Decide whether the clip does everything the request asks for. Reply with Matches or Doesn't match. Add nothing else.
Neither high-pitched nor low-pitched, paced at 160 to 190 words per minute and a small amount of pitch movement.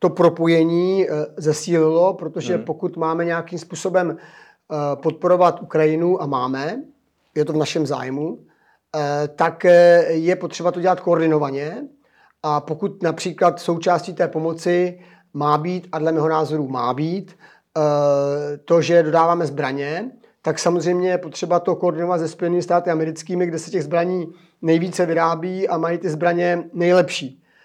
Doesn't match